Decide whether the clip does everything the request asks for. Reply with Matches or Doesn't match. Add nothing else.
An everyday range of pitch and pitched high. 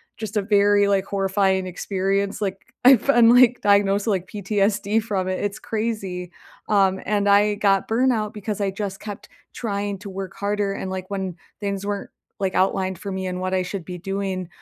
Doesn't match